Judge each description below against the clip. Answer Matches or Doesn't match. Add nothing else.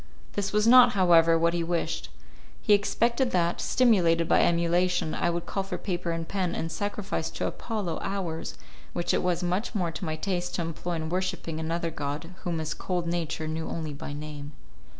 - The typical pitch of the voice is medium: Matches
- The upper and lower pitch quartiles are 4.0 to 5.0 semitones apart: Doesn't match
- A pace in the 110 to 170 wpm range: Doesn't match